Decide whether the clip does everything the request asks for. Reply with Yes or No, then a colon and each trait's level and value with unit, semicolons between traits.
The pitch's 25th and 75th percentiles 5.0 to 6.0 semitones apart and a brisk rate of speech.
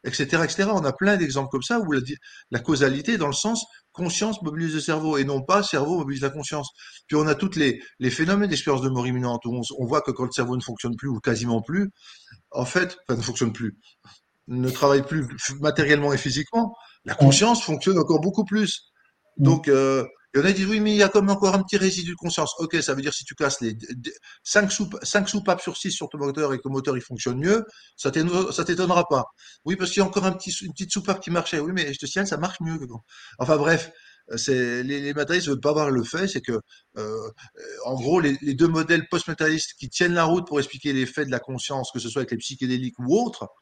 Yes: wide, 5.6 semitones; fast, 250 wpm